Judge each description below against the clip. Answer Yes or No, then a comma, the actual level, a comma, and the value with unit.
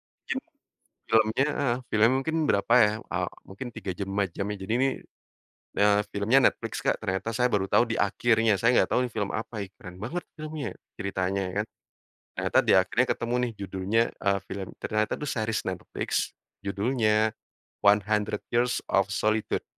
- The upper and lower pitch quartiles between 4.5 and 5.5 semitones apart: No, average, 3.3 semitones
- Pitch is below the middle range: Yes, low, 110 Hz